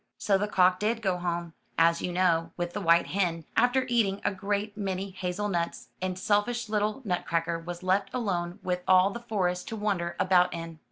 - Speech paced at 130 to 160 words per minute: No, average, 190 wpm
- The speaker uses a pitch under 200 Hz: Yes, medium, 185 Hz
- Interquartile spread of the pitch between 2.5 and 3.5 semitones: Yes, average, 3.0 semitones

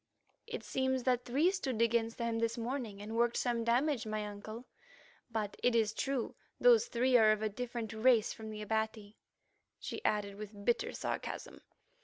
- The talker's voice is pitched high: Yes, high, 230 Hz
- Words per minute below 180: Yes, average, 170 wpm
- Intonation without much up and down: Yes, narrow, 2.3 semitones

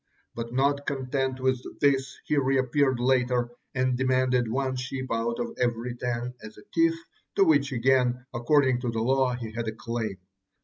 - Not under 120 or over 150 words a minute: No, average, 170 wpm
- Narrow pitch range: Yes, narrow, 1.9 semitones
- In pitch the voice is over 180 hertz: No, low, 130 Hz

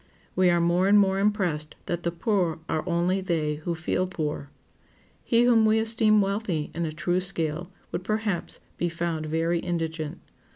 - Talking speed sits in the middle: Yes, average, 170 wpm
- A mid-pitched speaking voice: Yes, medium, 175 Hz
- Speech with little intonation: No, average, 3.2 semitones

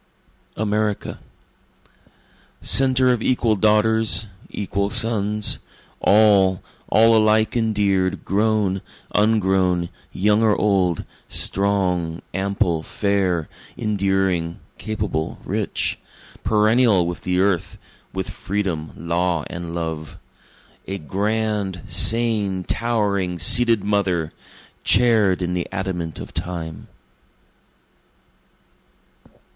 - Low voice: Yes, low, 100 Hz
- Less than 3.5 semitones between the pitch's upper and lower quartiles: Yes, average, 3.1 semitones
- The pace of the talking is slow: Yes, slow, 85 wpm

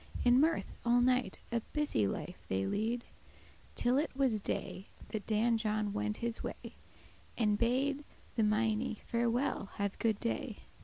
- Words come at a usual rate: Yes, average, 150 wpm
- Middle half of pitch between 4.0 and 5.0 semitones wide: No, average, 2.9 semitones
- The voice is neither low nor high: No, high, 230 Hz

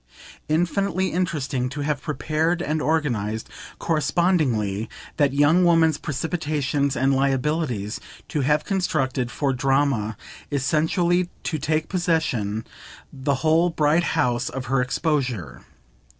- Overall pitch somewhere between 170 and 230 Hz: No, medium, 145 Hz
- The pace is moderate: No, slow, 110 wpm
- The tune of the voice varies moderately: Yes, average, 3.7 semitones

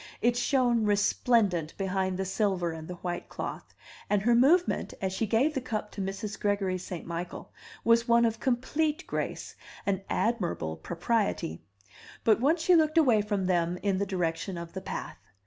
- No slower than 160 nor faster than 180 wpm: Yes, average, 170 wpm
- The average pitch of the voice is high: Yes, high, 205 Hz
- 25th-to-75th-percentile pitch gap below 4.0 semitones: No, average, 4.4 semitones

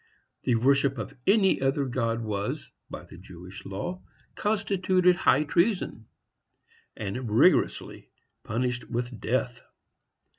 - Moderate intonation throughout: No, wide, 7.9 semitones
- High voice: No, low, 125 Hz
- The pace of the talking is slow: Yes, slow, 110 wpm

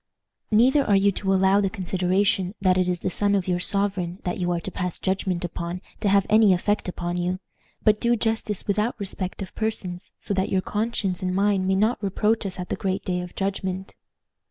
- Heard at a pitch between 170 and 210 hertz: Yes, high, 190 Hz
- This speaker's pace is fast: Yes, fast, 210 wpm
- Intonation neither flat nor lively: No, narrow, 2.1 semitones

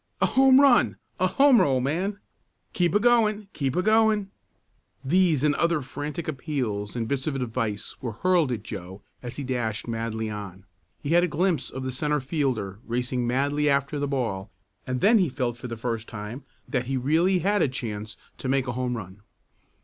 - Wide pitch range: Yes, wide, 6.4 semitones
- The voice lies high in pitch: No, low, 135 Hz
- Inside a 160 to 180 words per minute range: No, average, 190 wpm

